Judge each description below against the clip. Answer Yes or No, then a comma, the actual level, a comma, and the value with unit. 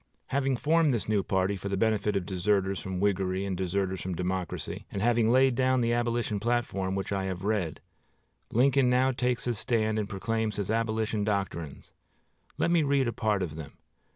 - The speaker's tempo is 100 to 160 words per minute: No, average, 185 wpm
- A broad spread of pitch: No, average, 3.9 semitones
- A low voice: Yes, low, 105 Hz